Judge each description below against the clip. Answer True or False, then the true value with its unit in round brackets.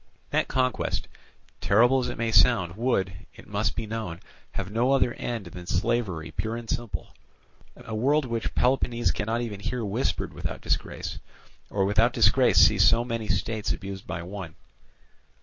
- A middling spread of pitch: True (3.5 semitones)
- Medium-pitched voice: False (110 Hz)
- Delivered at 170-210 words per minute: False (160 wpm)